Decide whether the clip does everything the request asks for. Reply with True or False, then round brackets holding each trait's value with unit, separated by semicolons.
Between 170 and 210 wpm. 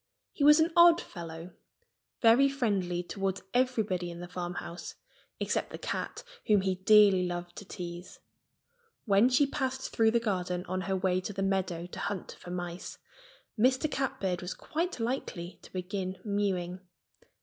False (155 wpm)